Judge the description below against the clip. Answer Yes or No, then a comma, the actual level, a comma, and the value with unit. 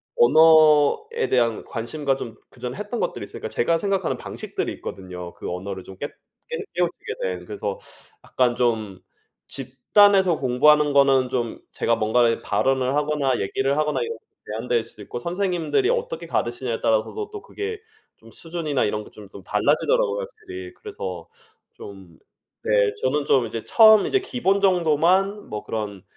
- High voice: No, medium, 140 Hz